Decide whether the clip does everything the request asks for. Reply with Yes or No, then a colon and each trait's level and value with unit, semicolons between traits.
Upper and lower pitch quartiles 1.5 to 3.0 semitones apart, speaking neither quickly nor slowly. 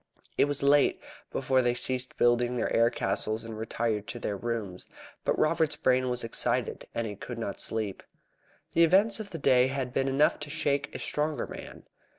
No: average, 4.0 semitones; average, 185 wpm